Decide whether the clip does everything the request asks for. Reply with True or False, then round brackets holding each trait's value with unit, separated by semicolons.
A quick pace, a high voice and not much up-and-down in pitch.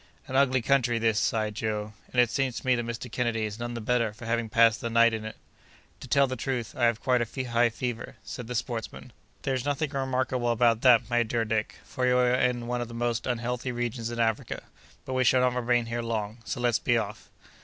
False (235 wpm; 120 Hz; 1.6 semitones)